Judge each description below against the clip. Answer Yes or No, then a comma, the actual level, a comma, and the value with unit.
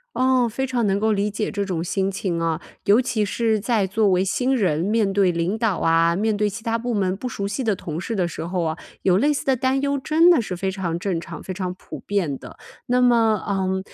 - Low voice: No, high, 200 Hz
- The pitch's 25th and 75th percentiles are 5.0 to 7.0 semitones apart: No, average, 4.0 semitones